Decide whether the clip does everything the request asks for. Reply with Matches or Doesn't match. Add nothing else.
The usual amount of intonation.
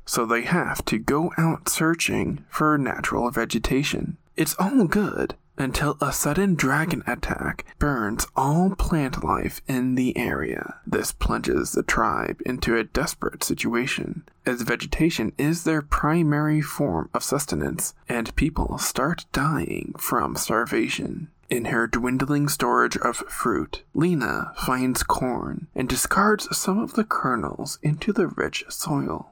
Matches